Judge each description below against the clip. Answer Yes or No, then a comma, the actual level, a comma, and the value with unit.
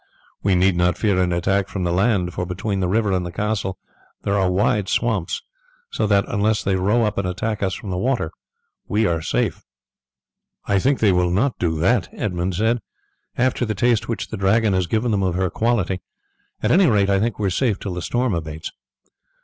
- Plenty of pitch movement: No, average, 3.3 semitones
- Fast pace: Yes, fast, 215 wpm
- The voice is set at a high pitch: No, low, 100 Hz